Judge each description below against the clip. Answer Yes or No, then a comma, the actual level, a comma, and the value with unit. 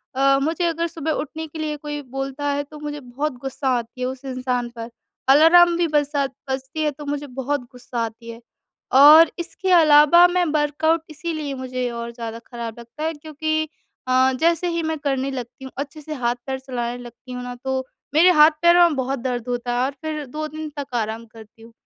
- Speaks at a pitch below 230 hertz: No, very high, 280 Hz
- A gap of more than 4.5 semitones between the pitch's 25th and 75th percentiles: No, average, 3.9 semitones